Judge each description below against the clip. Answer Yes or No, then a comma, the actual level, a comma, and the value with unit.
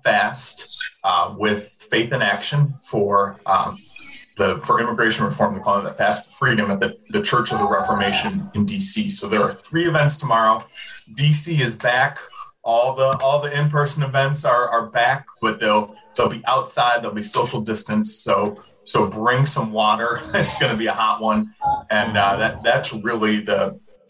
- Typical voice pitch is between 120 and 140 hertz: Yes, low, 135 Hz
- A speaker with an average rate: Yes, average, 185 wpm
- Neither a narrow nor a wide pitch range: No, wide, 8.9 semitones